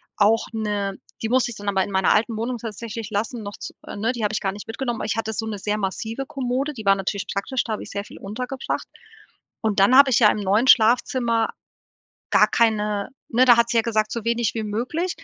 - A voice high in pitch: Yes, high, 225 Hz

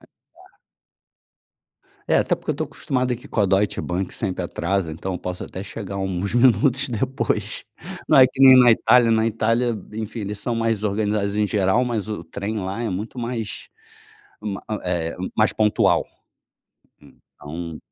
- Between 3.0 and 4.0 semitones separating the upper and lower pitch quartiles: Yes, average, 3.6 semitones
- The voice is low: Yes, low, 105 Hz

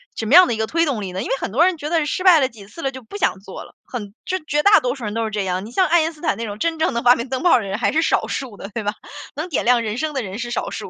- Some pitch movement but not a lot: No, wide, 6.7 semitones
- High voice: Yes, very high, 250 Hz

